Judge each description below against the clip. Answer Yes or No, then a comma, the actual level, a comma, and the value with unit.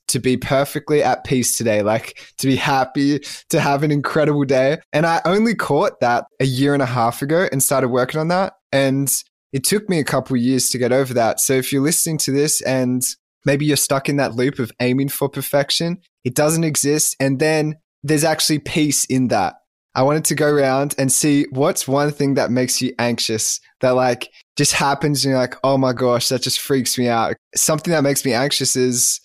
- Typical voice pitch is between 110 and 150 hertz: Yes, medium, 140 Hz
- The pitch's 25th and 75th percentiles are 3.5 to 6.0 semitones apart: No, average, 2.7 semitones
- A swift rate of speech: Yes, fast, 215 wpm